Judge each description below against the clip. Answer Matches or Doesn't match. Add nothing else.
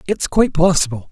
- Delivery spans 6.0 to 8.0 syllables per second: Matches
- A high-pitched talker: Doesn't match